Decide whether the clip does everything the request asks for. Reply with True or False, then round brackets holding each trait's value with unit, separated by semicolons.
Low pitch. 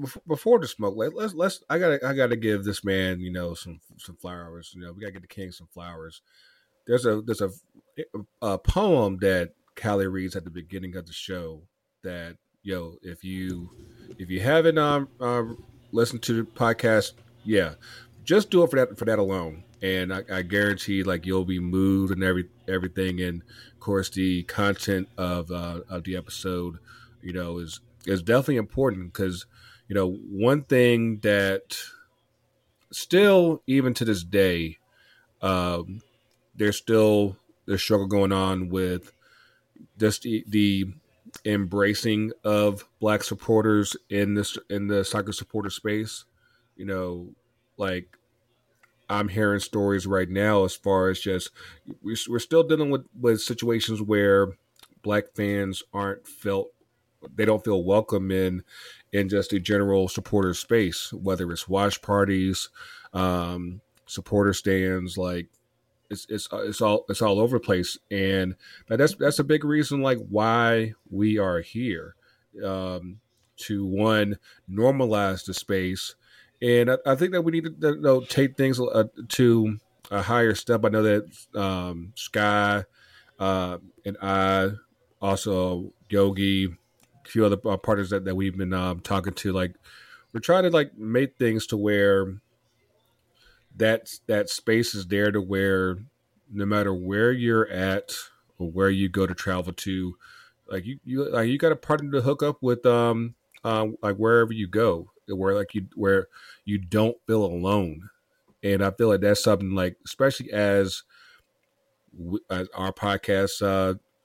True (100 Hz)